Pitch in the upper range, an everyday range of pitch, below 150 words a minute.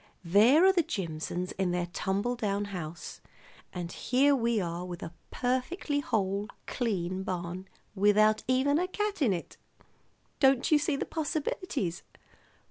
No: high, 210 Hz; wide, 7.4 semitones; average, 140 wpm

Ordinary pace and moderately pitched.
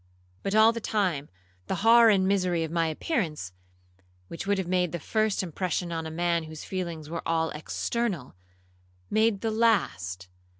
Yes: average, 170 wpm; medium, 180 Hz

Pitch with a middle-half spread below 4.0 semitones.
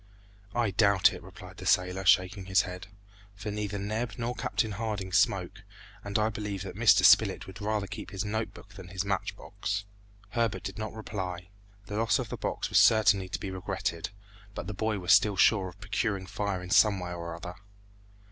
Yes: narrow, 2.4 semitones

